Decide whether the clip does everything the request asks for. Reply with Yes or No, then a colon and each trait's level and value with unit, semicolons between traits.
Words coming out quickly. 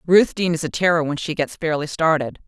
Yes: fast, 240 wpm